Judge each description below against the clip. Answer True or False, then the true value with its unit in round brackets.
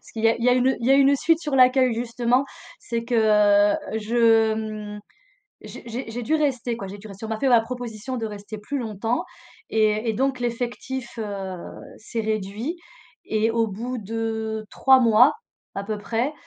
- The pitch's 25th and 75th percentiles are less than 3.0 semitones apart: True (2.6 semitones)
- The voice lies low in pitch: False (230 Hz)